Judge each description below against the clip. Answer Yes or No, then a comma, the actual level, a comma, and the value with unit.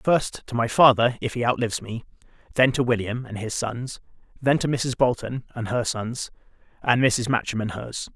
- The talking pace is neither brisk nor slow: Yes, average, 190 wpm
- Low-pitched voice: Yes, low, 120 Hz